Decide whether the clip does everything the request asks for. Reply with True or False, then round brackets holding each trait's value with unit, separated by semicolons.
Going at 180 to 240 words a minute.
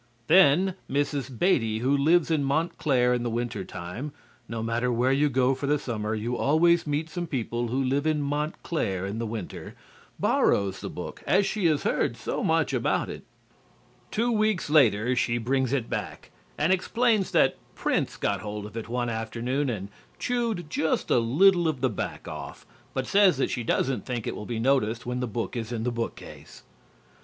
True (185 wpm)